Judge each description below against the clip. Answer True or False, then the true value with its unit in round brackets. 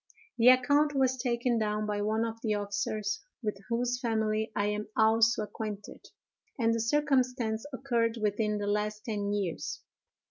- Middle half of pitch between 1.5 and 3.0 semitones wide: True (2.5 semitones)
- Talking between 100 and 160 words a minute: True (150 wpm)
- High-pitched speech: True (220 Hz)